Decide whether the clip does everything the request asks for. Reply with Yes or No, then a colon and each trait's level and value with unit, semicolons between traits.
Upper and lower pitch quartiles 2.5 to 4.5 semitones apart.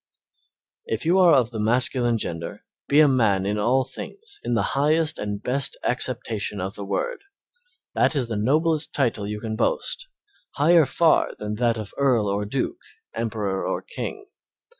No: average, 5.1 semitones